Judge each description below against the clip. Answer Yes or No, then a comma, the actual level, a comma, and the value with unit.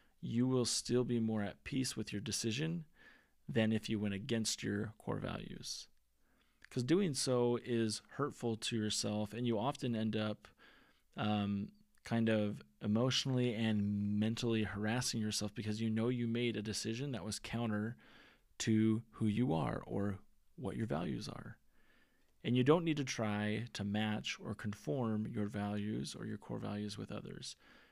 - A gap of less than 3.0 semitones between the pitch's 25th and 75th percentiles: Yes, narrow, 2.4 semitones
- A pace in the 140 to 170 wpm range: Yes, average, 160 wpm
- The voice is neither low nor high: No, low, 110 Hz